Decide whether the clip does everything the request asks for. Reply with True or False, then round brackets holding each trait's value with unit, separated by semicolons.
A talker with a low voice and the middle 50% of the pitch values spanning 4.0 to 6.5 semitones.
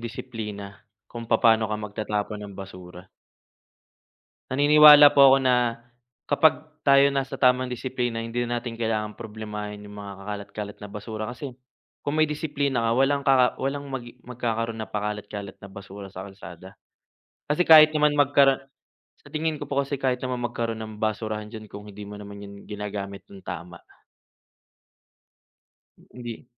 True (115 Hz; 4.5 semitones)